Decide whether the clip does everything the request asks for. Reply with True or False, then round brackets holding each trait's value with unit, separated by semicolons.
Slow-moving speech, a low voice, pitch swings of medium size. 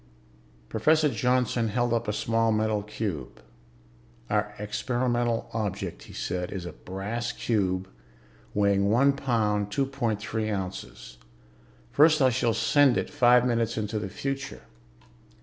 True (130 wpm; 110 Hz; 3.3 semitones)